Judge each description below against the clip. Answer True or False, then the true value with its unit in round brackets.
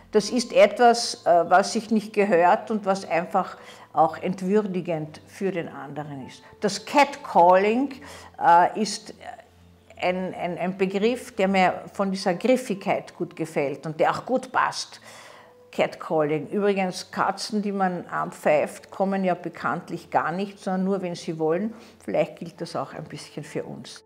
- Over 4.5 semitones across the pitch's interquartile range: False (3.7 semitones)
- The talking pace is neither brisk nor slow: True (145 wpm)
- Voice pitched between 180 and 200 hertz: True (190 Hz)